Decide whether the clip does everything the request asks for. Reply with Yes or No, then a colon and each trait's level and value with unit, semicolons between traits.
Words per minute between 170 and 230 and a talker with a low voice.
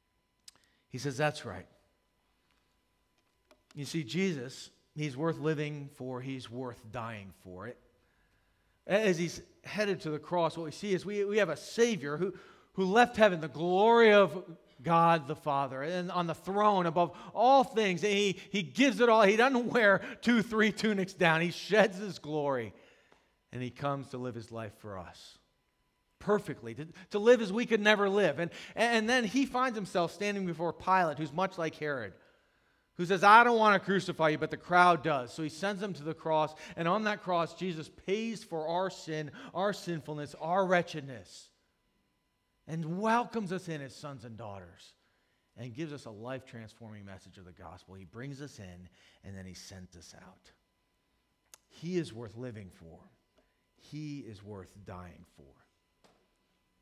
No: average, 175 wpm; medium, 165 Hz